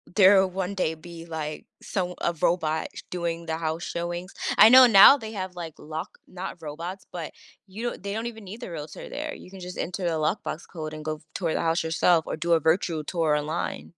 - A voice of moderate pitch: Yes, medium, 175 Hz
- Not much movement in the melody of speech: No, average, 3.0 semitones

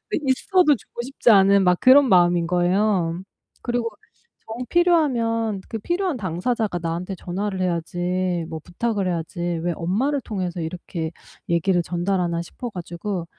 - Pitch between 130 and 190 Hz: Yes, medium, 185 Hz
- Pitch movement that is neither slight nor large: Yes, average, 4.9 semitones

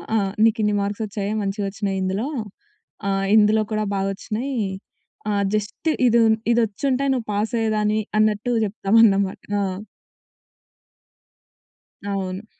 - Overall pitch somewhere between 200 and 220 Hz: Yes, high, 210 Hz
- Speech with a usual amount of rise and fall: No, narrow, 2.1 semitones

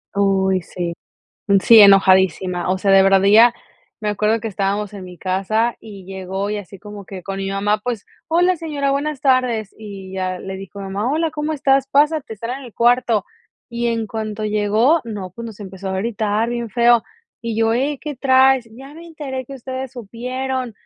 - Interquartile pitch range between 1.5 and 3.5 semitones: No, average, 4.9 semitones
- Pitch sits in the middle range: No, high, 220 Hz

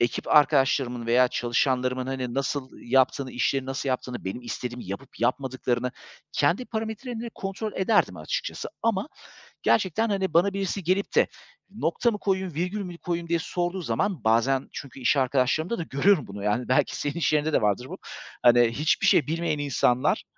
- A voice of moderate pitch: Yes, medium, 145 Hz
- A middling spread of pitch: No, wide, 6.8 semitones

